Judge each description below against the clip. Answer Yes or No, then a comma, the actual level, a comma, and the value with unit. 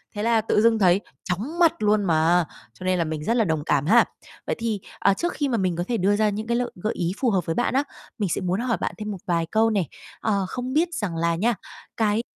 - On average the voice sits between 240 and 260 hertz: No, high, 210 Hz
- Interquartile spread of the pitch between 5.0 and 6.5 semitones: No, average, 4.6 semitones